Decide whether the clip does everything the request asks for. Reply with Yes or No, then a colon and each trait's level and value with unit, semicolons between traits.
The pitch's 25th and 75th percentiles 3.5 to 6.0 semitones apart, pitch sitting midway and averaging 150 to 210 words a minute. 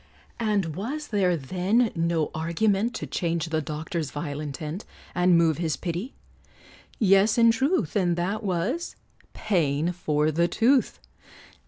No: average, 4.9 semitones; medium, 175 Hz; slow, 135 wpm